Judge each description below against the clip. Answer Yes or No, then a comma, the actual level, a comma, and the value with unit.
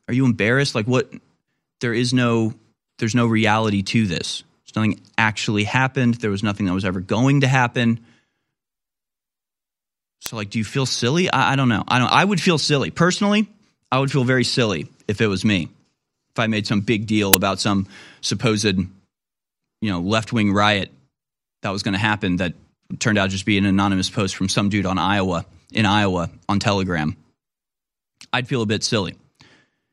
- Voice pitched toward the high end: No, low, 110 Hz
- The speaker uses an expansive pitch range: No, average, 3.7 semitones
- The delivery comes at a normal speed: Yes, average, 185 wpm